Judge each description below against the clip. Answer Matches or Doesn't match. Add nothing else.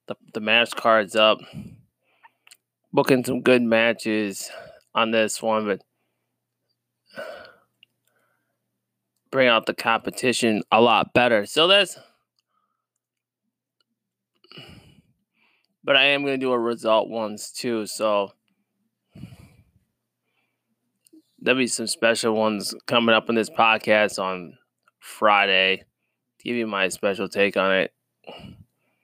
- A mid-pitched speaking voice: Doesn't match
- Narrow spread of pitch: Doesn't match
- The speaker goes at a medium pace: Doesn't match